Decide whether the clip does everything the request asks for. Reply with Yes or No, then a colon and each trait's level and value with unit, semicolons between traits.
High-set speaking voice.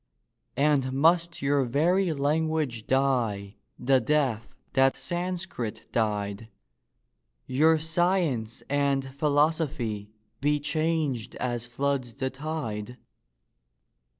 No: medium, 140 Hz